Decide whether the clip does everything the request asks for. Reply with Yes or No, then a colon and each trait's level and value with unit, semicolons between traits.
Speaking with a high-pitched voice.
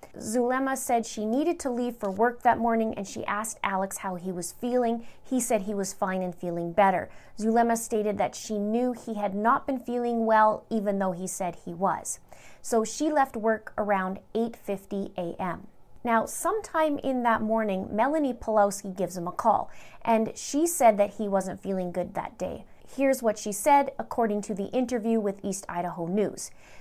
Yes: high, 220 Hz